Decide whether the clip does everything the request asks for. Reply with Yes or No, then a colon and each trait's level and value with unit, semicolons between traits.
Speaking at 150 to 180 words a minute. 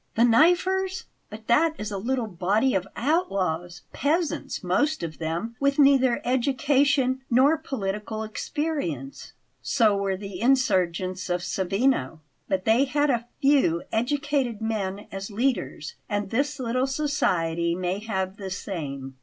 No: slow, 135 wpm